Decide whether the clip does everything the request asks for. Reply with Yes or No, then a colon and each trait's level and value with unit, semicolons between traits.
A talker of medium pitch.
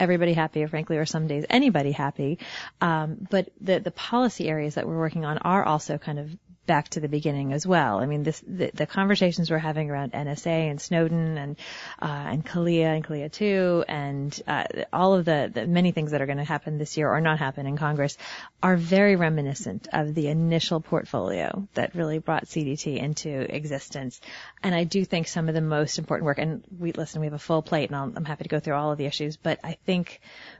Yes: medium, 155 Hz